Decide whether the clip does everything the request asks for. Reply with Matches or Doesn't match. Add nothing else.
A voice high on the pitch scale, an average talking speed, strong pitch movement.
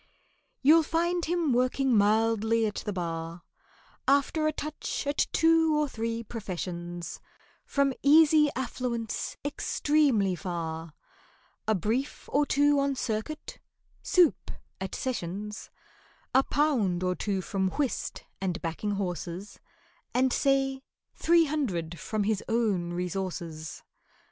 Doesn't match